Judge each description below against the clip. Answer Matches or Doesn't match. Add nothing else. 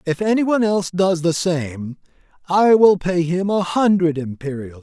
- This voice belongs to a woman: Doesn't match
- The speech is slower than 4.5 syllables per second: Doesn't match